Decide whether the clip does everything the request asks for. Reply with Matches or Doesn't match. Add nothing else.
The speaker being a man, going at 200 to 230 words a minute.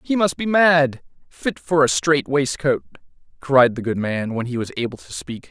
Matches